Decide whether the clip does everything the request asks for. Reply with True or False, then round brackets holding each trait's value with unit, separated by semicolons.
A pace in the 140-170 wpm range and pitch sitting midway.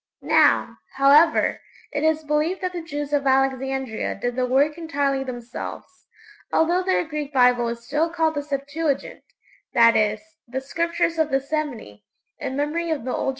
False (165 wpm; 285 Hz)